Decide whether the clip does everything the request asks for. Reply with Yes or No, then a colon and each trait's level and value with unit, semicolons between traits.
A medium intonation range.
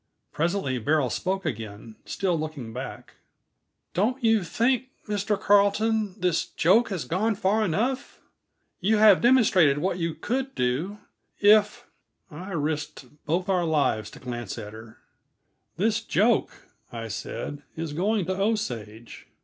No: wide, 6.6 semitones